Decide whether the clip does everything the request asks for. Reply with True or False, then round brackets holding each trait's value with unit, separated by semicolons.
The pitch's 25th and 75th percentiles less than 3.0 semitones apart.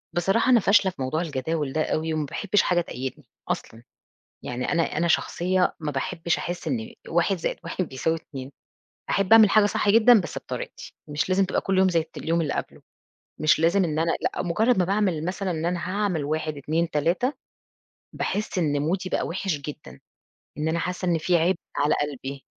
False (3.6 semitones)